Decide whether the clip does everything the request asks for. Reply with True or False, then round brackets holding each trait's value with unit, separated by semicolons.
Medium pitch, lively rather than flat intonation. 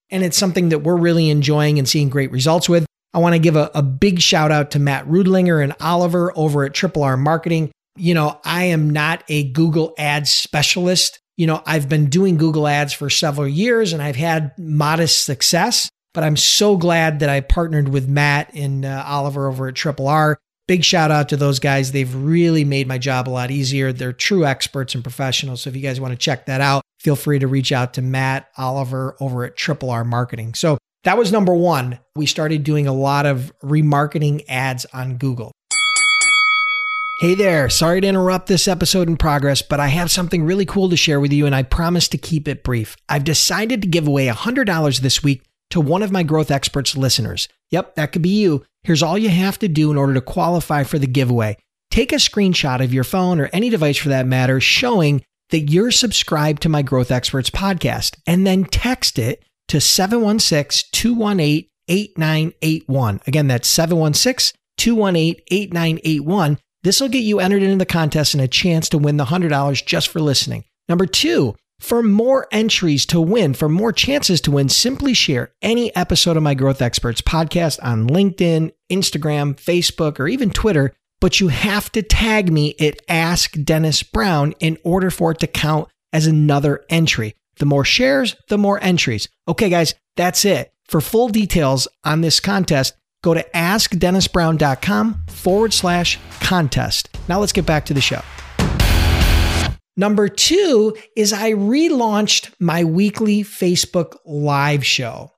False (160 Hz; 4.8 semitones)